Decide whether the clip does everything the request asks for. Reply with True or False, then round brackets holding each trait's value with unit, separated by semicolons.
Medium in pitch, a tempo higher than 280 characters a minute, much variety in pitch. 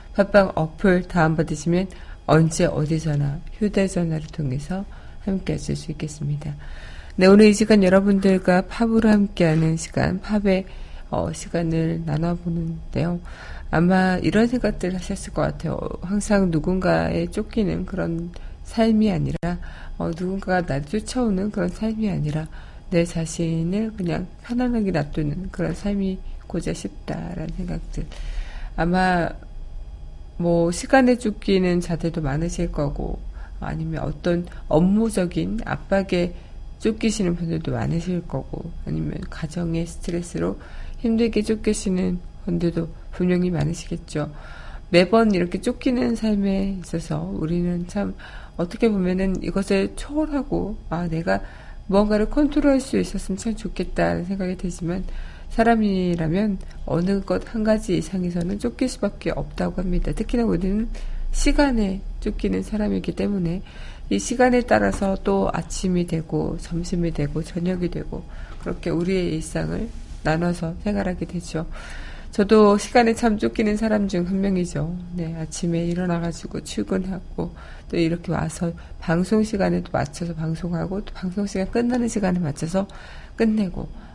False (180 Hz; 300 characters per minute; 3.7 semitones)